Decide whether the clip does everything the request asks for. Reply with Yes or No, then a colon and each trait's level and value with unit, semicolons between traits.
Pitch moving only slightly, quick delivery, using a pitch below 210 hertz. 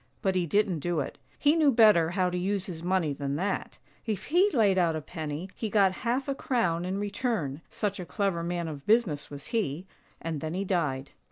No: average, 4.5 semitones; fast, 225 wpm; medium, 185 Hz